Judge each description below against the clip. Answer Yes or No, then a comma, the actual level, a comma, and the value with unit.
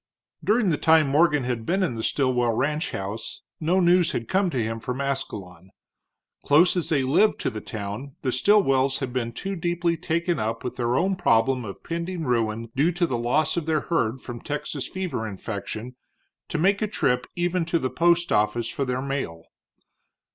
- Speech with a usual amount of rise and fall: No, wide, 6.5 semitones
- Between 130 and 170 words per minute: No, average, 185 wpm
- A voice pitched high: No, low, 135 Hz